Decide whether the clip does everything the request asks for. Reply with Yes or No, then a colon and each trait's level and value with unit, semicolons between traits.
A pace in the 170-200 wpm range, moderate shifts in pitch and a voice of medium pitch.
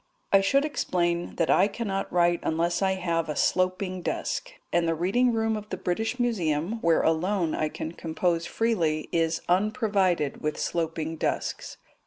No: average, 160 wpm; average, 3.9 semitones; medium, 180 Hz